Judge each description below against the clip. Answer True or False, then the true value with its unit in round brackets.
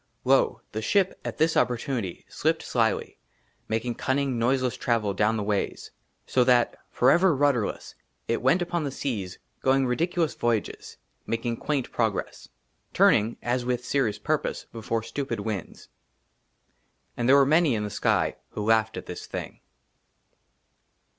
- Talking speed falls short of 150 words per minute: True (140 wpm)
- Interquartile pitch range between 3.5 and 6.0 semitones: True (3.8 semitones)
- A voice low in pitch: True (120 Hz)